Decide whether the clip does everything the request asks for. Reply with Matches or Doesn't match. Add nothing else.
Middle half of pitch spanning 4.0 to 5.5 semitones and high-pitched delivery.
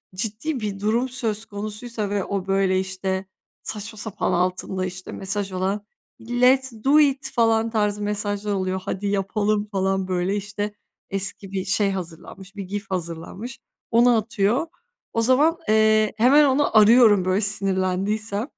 Doesn't match